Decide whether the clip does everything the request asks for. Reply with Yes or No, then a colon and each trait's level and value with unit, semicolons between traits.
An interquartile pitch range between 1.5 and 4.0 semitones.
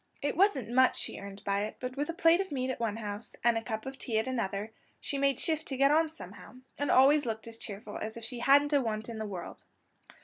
No: average, 4.5 semitones